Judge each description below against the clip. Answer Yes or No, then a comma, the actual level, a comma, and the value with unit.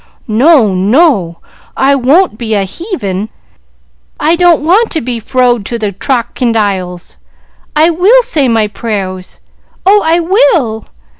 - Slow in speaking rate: Yes, slow, 130 wpm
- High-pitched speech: Yes, very high, 250 Hz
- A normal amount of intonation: No, wide, 8.3 semitones